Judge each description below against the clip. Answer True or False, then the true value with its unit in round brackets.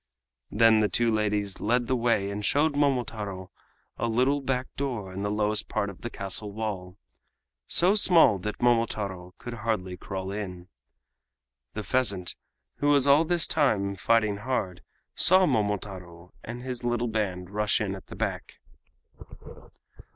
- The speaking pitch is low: True (110 Hz)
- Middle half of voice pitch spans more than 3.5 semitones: True (3.9 semitones)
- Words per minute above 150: False (145 wpm)